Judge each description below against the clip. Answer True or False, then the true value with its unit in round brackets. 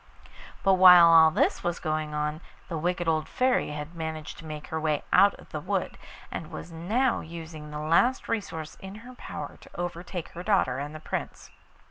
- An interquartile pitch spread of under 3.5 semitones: True (2.9 semitones)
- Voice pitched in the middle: True (165 Hz)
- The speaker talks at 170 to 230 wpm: True (190 wpm)